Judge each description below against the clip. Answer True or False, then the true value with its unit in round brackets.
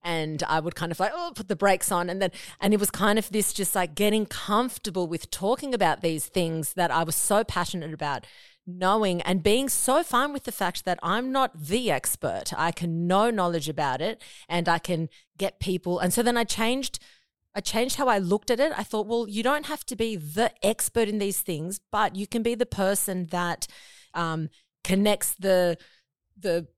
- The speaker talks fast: True (210 wpm)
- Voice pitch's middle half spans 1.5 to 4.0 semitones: False (4.5 semitones)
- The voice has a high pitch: True (195 Hz)